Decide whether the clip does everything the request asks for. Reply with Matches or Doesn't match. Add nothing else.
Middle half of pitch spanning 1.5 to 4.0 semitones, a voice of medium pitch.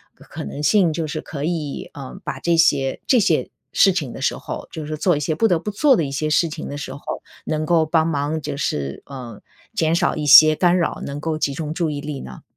Matches